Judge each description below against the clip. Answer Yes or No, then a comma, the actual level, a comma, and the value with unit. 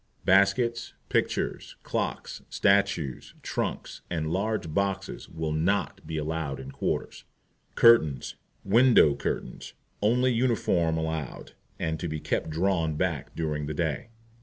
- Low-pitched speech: Yes, very low, 80 Hz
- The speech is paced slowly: Yes, slow, 120 wpm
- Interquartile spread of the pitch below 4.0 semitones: No, average, 4.3 semitones